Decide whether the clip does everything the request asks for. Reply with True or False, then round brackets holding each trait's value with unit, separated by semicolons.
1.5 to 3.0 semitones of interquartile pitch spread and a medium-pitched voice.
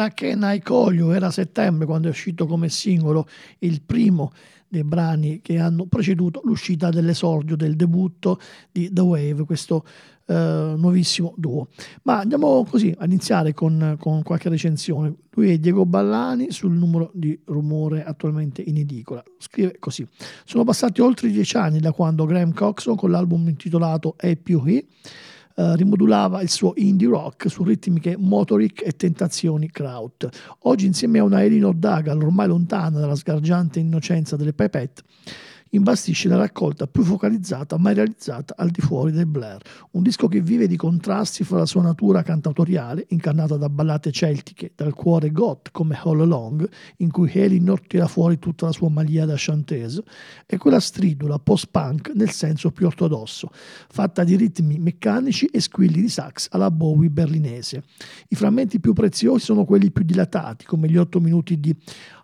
False (3.8 semitones; 170 Hz)